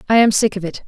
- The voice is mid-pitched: No, high, 205 Hz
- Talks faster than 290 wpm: Yes, fast, 345 wpm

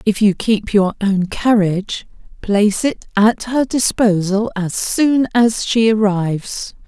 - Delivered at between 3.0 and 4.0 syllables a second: Yes, 3.8 syllables/s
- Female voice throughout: Yes, female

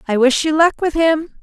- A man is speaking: No, female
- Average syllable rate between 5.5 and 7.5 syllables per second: No, 5.0 syllables/s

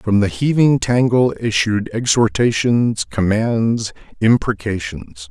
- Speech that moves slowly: Yes, slow, 90 wpm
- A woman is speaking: No, male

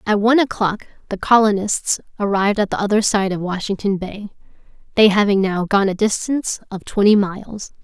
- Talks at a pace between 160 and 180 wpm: Yes, average, 170 wpm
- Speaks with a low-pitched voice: No, high, 205 Hz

